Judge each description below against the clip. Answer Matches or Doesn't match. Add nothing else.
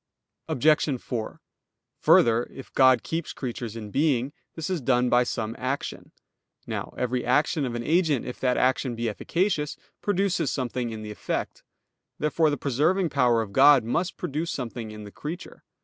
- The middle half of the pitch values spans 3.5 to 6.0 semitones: Matches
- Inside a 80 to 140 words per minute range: Doesn't match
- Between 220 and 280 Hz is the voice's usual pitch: Doesn't match